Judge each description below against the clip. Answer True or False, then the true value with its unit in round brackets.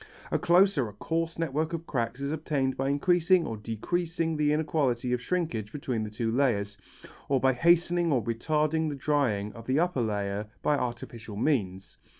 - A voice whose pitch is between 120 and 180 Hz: True (140 Hz)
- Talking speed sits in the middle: True (175 wpm)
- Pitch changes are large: True (5.9 semitones)